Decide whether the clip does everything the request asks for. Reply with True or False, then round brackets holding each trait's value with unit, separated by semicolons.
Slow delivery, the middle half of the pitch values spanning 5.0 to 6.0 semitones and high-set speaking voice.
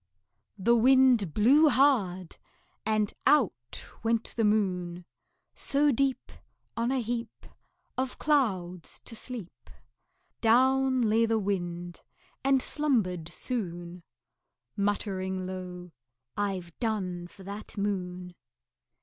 True (100 wpm; 5.4 semitones; 210 Hz)